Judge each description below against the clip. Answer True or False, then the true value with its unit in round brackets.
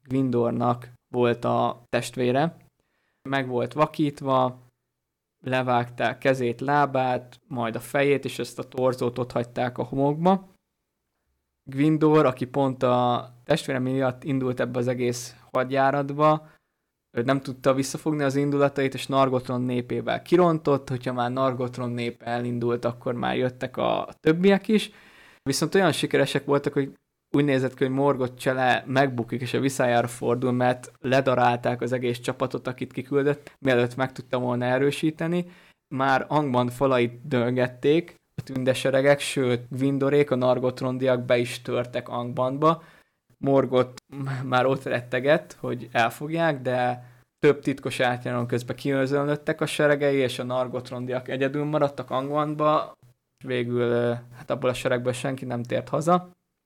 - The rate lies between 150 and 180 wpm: False (130 wpm)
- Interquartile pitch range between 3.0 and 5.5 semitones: False (2.4 semitones)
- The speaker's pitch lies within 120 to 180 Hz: True (130 Hz)